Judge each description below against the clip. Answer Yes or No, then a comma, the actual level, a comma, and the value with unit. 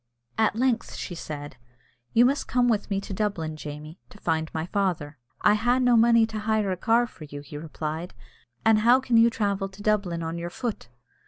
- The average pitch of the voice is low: No, high, 200 Hz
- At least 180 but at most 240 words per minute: Yes, average, 200 wpm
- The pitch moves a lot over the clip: Yes, wide, 6.0 semitones